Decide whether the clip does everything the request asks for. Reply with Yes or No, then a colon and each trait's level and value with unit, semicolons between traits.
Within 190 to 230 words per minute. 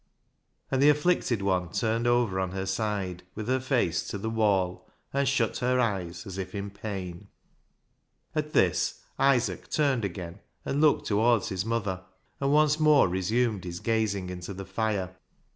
No: average, 160 wpm